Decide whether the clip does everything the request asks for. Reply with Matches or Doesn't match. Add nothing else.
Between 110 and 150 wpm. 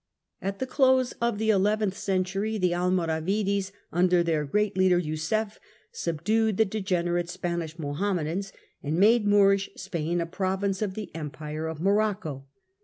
Matches